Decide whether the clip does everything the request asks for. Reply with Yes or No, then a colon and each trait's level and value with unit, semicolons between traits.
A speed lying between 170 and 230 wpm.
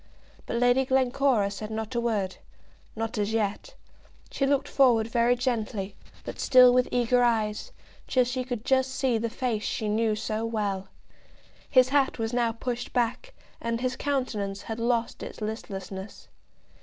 No: average, 155 wpm